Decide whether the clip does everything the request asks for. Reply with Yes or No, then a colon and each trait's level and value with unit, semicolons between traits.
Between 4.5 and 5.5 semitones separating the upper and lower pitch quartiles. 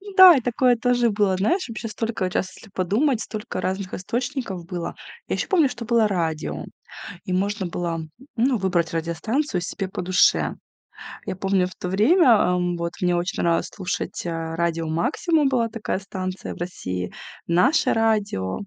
Yes: average, 5.2 semitones